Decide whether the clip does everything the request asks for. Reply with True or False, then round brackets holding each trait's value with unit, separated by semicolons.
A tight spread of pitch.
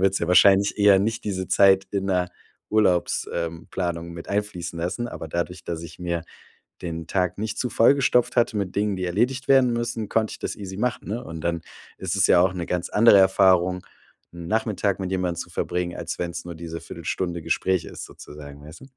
False (3.3 semitones)